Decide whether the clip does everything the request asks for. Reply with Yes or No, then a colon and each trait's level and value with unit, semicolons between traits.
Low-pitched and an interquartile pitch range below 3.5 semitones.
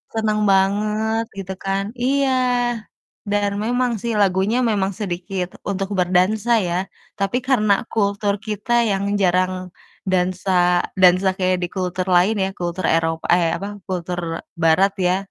No: high, 195 Hz; average, 2.7 semitones